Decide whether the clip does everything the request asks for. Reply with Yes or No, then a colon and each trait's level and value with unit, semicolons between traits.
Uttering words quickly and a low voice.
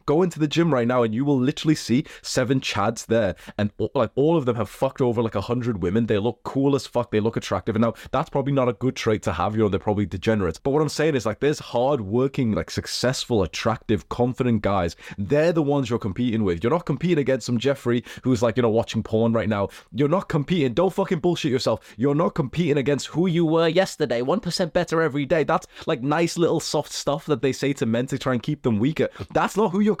Yes: fast, 245 wpm; low, 130 Hz